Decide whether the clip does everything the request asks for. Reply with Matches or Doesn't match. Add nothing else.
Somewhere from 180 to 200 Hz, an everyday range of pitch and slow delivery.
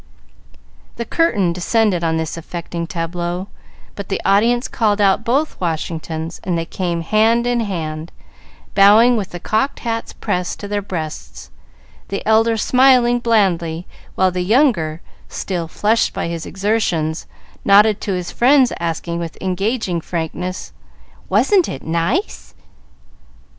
Matches